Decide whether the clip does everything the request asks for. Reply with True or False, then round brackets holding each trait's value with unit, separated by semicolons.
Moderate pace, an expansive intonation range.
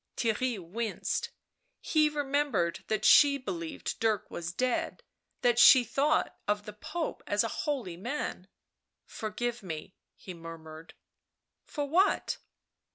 False (130 wpm; 7.5 semitones)